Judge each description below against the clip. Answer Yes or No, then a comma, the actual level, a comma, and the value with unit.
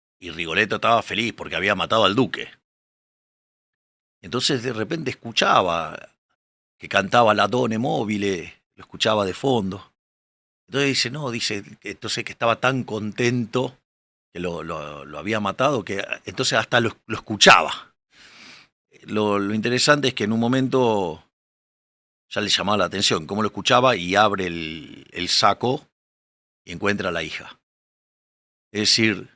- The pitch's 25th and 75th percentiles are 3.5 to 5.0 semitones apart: Yes, average, 4.7 semitones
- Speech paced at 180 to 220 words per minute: No, average, 145 wpm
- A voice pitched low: Yes, low, 110 Hz